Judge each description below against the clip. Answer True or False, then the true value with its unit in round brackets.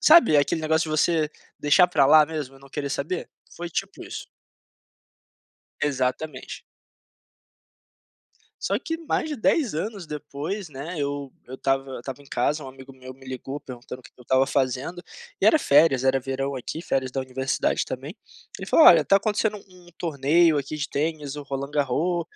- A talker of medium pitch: True (145 Hz)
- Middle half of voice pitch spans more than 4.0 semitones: False (3.7 semitones)